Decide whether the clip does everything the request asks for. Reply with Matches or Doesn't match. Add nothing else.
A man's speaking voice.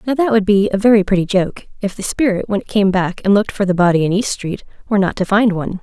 Doesn't match